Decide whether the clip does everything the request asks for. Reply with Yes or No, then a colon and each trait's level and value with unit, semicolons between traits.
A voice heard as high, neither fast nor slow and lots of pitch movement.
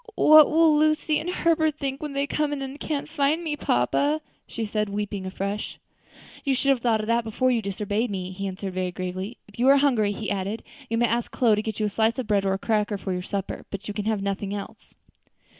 No: high, 220 Hz; fast, 240 wpm; wide, 5.7 semitones